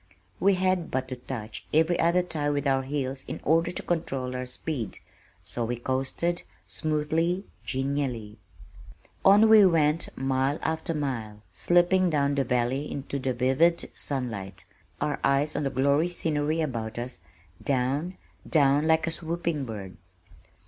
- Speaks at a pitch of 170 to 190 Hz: No, medium, 145 Hz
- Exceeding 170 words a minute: No, average, 145 wpm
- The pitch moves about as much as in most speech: Yes, average, 4.2 semitones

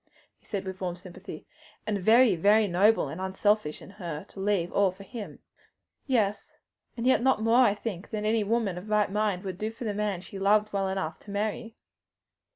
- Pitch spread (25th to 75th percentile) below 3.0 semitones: Yes, narrow, 2.4 semitones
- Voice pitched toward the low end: No, high, 205 Hz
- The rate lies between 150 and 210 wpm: Yes, average, 195 wpm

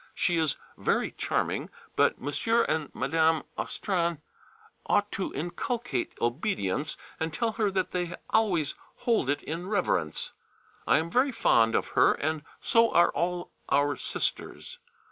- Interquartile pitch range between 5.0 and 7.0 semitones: Yes, average, 5.3 semitones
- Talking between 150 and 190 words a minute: No, average, 140 wpm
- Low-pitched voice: No, medium, 170 Hz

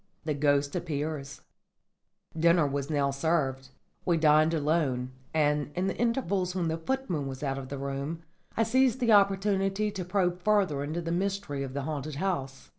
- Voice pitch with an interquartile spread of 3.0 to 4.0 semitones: No, average, 5.3 semitones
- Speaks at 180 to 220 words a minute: No, average, 170 wpm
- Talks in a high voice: No, medium, 160 Hz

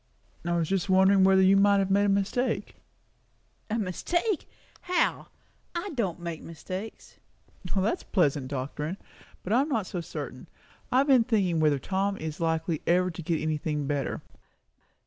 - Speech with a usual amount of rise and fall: Yes, average, 4.1 semitones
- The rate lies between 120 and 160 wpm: Yes, average, 150 wpm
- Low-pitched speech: No, high, 190 Hz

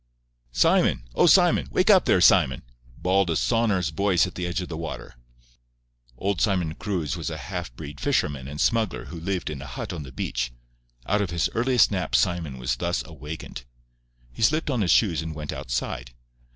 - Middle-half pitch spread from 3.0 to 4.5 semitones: No, wide, 5.5 semitones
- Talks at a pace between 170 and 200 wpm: Yes, average, 180 wpm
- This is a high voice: No, very low, 85 Hz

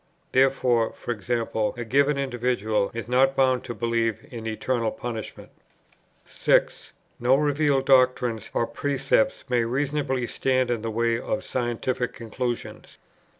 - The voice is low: Yes, low, 125 Hz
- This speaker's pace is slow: Yes, slow, 125 wpm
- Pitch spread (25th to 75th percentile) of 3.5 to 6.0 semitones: No, narrow, 2.4 semitones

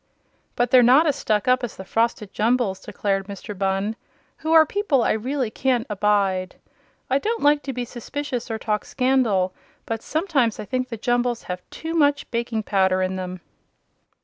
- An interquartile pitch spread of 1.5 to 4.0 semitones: No, average, 4.7 semitones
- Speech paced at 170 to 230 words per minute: Yes, average, 175 wpm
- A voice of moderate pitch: No, high, 235 Hz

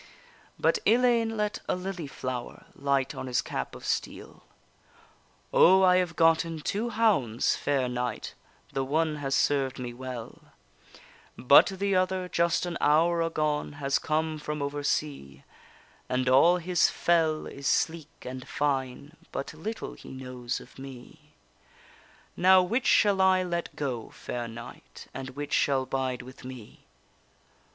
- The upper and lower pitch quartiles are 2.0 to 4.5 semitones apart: No, average, 5.3 semitones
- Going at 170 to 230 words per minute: No, average, 145 wpm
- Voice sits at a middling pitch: Yes, medium, 150 Hz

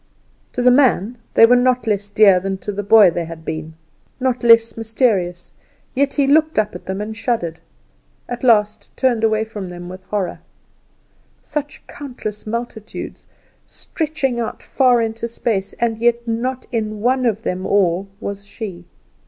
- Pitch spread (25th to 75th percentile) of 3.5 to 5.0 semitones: Yes, average, 3.8 semitones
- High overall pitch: Yes, high, 220 Hz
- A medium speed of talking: Yes, average, 160 wpm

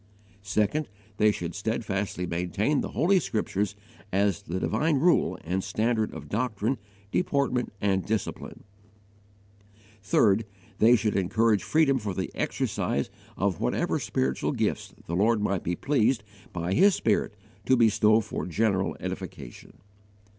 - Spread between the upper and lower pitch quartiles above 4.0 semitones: No, average, 3.5 semitones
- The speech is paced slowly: Yes, slow, 130 wpm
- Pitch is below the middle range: Yes, low, 105 Hz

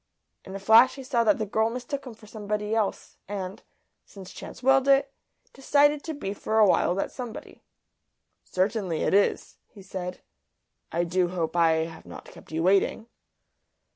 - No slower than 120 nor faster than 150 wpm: No, average, 170 wpm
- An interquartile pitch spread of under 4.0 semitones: No, average, 4.8 semitones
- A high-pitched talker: Yes, high, 210 Hz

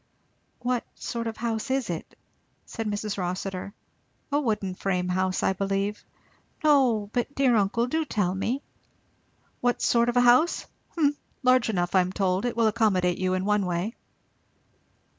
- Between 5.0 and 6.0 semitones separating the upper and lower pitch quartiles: No, average, 4.5 semitones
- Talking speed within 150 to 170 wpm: Yes, average, 160 wpm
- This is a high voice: Yes, high, 215 Hz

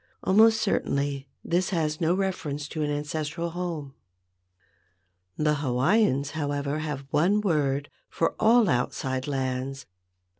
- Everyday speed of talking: No, slow, 115 wpm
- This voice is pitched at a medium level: Yes, medium, 150 Hz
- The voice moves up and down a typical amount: Yes, average, 4.0 semitones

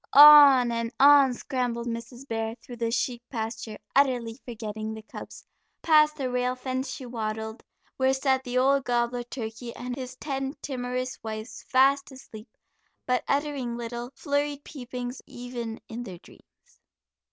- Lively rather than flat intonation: No, narrow, 2.5 semitones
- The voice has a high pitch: Yes, very high, 250 Hz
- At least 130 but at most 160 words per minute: Yes, average, 145 wpm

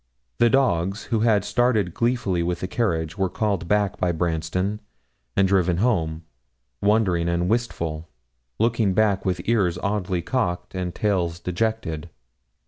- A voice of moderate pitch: No, very low, 95 Hz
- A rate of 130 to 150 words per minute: Yes, slow, 135 wpm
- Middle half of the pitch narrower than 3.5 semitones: No, average, 4.0 semitones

